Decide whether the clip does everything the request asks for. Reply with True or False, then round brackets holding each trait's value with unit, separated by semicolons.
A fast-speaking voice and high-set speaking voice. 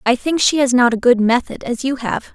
True (280 wpm; 250 Hz)